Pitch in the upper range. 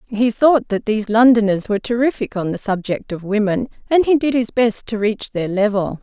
Yes: high, 220 Hz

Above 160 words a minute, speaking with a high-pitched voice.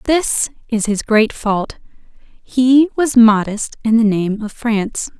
No: average, 150 wpm; high, 230 Hz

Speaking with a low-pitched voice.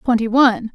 No: high, 235 Hz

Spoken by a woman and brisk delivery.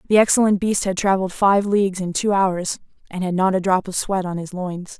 Yes: female; fast, 240 wpm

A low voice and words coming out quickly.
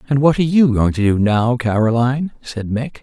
Yes: low, 125 Hz; fast, 220 wpm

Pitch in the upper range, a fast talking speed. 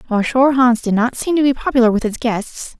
Yes: high, 245 Hz; fast, 255 wpm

